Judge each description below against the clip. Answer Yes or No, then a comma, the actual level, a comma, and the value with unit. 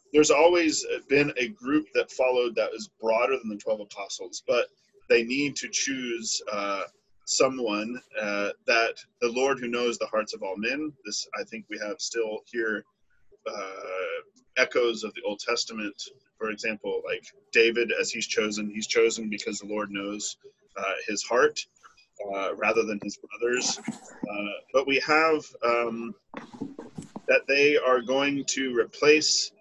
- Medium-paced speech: Yes, average, 155 wpm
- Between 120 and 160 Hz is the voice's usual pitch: Yes, low, 135 Hz